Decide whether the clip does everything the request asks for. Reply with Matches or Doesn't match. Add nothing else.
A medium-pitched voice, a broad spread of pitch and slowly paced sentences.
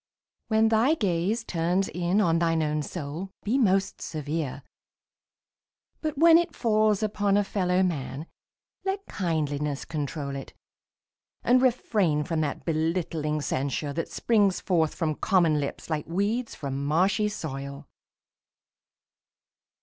Matches